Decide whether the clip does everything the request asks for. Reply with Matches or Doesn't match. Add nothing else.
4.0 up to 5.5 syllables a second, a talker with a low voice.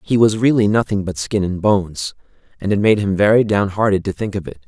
Doesn't match